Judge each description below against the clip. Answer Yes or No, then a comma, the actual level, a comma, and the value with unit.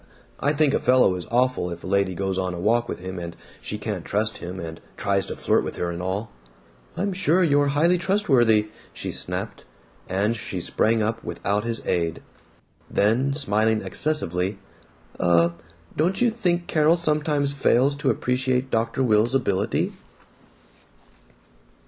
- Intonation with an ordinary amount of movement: No, wide, 6.8 semitones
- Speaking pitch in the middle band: No, low, 115 Hz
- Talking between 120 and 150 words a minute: No, average, 160 wpm